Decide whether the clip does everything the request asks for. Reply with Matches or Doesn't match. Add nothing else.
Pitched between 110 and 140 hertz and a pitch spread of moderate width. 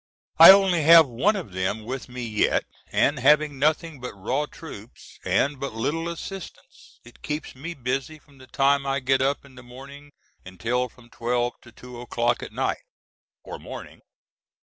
Matches